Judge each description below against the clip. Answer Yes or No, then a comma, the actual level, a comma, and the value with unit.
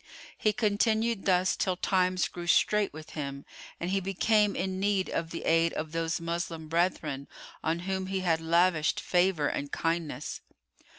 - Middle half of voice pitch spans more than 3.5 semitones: No, average, 2.8 semitones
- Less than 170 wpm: Yes, average, 160 wpm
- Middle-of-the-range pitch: Yes, medium, 175 Hz